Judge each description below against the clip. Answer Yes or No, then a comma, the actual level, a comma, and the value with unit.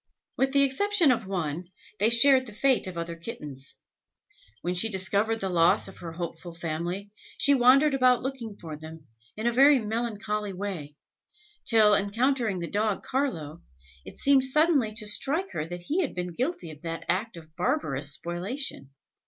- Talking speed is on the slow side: No, average, 170 wpm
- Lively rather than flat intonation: Yes, wide, 7.2 semitones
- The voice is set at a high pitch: Yes, high, 210 Hz